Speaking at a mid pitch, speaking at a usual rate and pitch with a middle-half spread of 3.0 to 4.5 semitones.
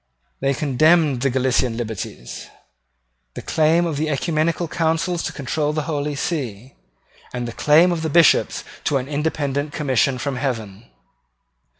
No: medium, 145 Hz; slow, 130 wpm; average, 3.7 semitones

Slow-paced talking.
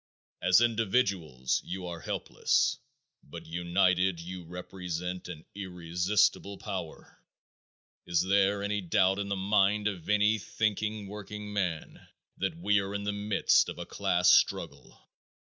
Yes: slow, 130 wpm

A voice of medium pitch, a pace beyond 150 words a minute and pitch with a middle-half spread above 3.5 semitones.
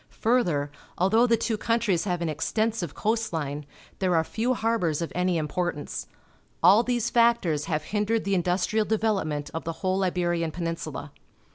Yes: medium, 180 Hz; average, 160 wpm; wide, 5.4 semitones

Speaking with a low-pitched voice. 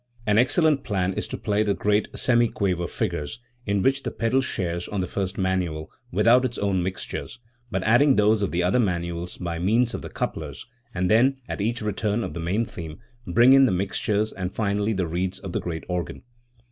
Yes: low, 100 Hz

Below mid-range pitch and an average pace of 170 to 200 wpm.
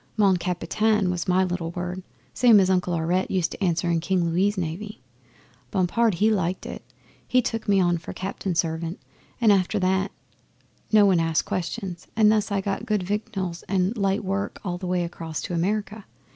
No: medium, 185 Hz; average, 185 wpm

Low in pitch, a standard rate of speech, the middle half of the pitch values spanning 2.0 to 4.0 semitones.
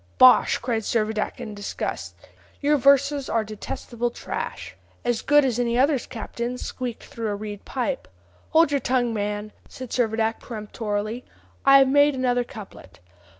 No: high, 235 Hz; average, 150 wpm; average, 3.5 semitones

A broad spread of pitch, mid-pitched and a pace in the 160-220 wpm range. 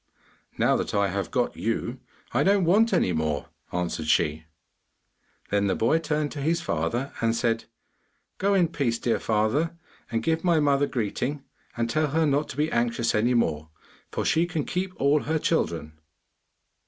No: wide, 6.8 semitones; low, 130 Hz; average, 170 wpm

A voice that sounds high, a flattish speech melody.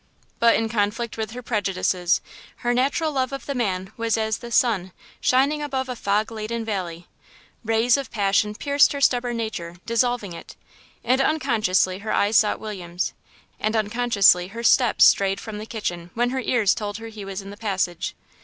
No: high, 220 Hz; average, 3.5 semitones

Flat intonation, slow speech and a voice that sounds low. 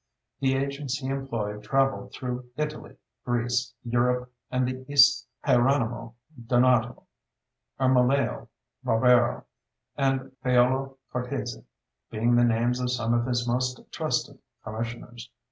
Yes: narrow, 1.8 semitones; slow, 110 wpm; low, 125 Hz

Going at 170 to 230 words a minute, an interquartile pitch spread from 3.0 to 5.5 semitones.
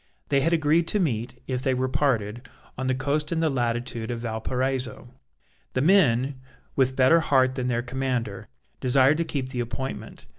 No: average, 175 wpm; narrow, 2.5 semitones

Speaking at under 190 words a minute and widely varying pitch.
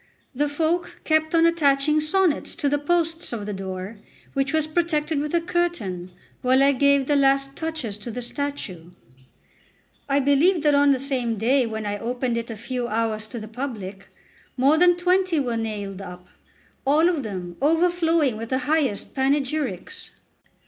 Yes: average, 170 wpm; wide, 5.7 semitones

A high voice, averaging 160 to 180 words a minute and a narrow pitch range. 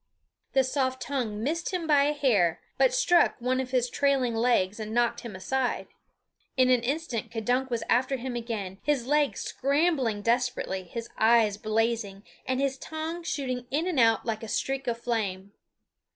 No: very high, 250 Hz; average, 170 wpm; average, 3.6 semitones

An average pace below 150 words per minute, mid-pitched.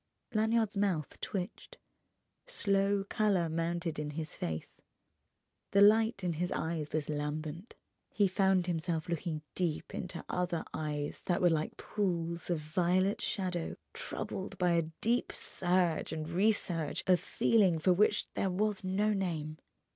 Yes: average, 140 wpm; medium, 180 Hz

